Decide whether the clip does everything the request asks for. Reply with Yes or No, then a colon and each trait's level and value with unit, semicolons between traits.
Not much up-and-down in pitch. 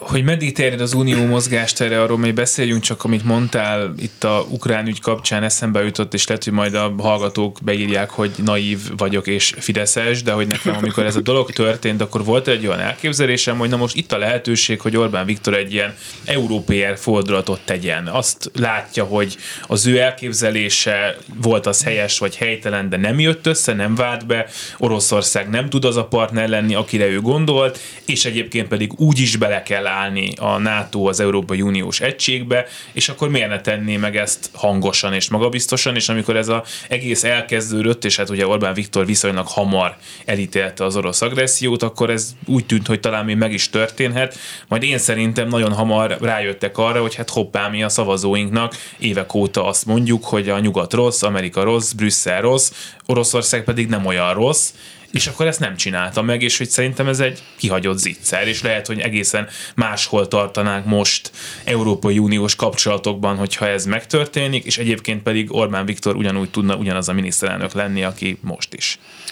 No: average, 3.0 semitones